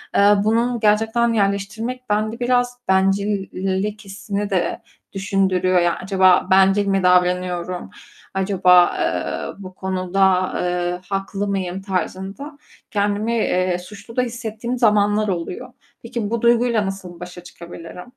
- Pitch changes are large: No, average, 3.1 semitones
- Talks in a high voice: Yes, high, 195 Hz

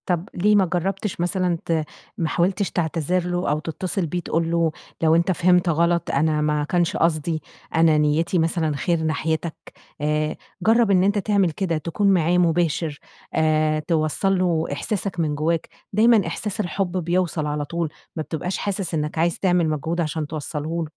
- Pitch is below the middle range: No, medium, 170 Hz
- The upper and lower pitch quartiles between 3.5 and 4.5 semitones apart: No, narrow, 2.6 semitones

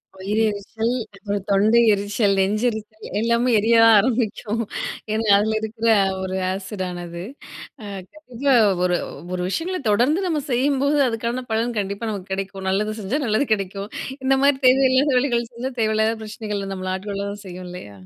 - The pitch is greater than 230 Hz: No, high, 220 Hz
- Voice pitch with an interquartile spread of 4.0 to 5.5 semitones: No, average, 3.3 semitones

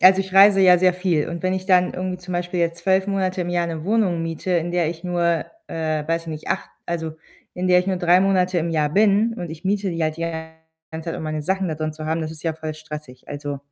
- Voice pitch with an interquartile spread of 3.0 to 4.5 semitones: No, narrow, 2.5 semitones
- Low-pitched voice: No, medium, 170 Hz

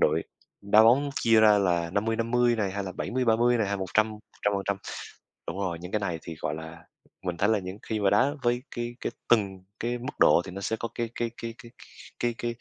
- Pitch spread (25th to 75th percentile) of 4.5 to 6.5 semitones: No, average, 3.7 semitones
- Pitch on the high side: No, low, 105 Hz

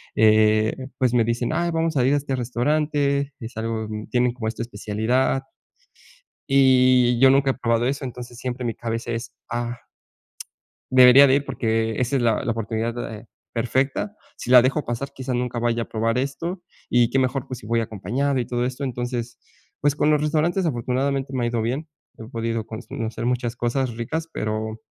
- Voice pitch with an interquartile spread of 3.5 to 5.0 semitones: No, average, 2.8 semitones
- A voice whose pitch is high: No, low, 125 Hz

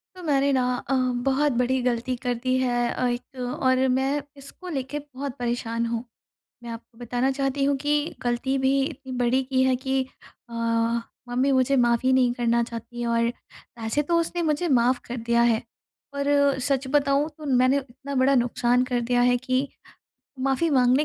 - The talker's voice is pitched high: Yes, very high, 260 Hz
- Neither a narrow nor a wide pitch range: No, narrow, 2.3 semitones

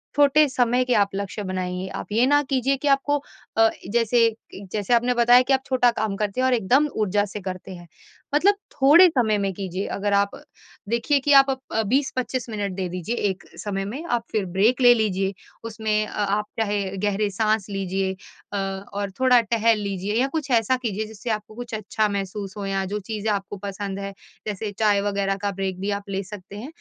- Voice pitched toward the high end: Yes, high, 210 Hz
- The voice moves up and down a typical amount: Yes, average, 3.7 semitones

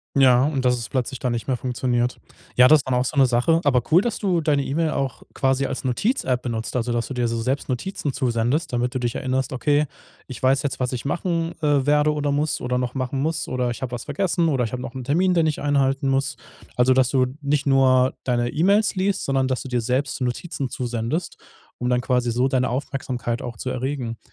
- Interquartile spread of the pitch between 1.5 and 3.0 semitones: Yes, average, 2.7 semitones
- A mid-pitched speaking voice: No, low, 130 Hz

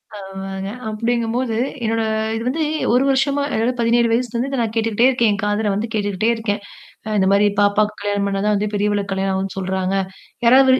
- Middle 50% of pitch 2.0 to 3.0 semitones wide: Yes, average, 2.7 semitones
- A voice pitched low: No, high, 215 Hz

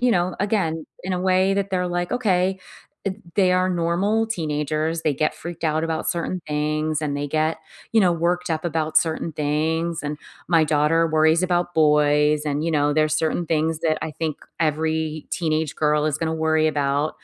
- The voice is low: No, medium, 160 Hz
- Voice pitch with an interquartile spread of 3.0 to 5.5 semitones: No, narrow, 2.5 semitones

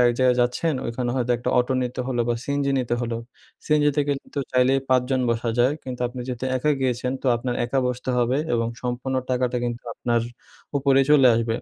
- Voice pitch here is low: Yes, low, 125 Hz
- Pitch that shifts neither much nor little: No, narrow, 1.7 semitones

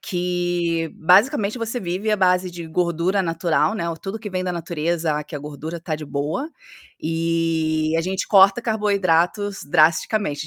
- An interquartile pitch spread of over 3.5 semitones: No, average, 3.1 semitones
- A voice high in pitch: No, medium, 175 Hz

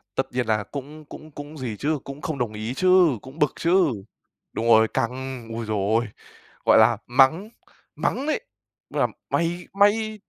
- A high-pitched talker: No, medium, 140 Hz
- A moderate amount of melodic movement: No, wide, 6.2 semitones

